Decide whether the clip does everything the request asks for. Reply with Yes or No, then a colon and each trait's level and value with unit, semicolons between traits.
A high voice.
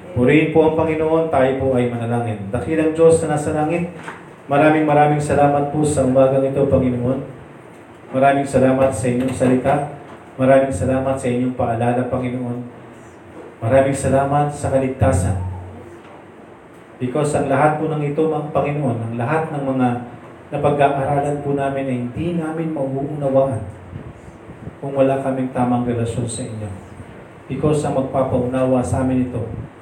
No: low, 135 Hz